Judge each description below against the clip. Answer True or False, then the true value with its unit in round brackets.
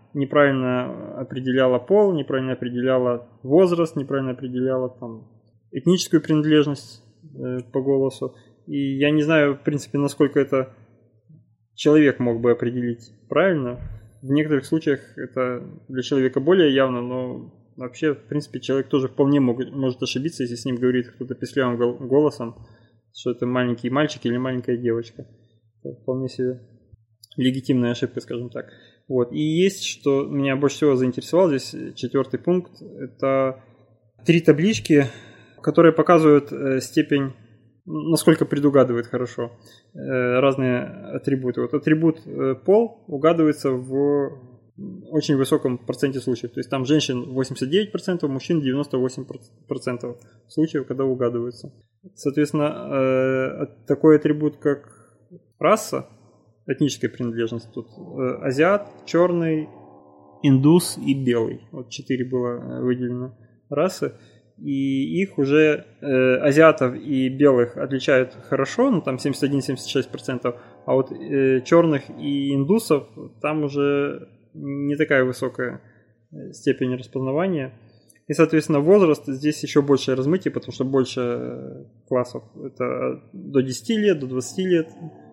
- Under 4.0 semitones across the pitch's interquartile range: True (3.2 semitones)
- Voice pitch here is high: False (135 Hz)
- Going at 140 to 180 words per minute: False (120 wpm)